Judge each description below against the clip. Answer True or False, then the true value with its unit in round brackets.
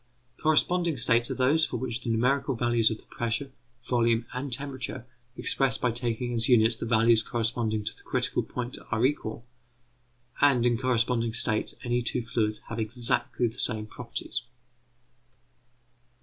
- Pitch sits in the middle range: False (120 Hz)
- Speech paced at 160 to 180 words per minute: False (150 wpm)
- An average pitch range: False (2.0 semitones)